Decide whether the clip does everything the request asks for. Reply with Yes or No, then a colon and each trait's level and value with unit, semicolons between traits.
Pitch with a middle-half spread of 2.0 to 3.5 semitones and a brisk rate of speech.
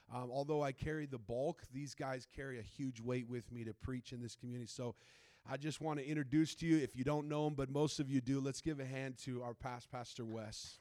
Yes: average, 3.0 semitones; fast, 255 wpm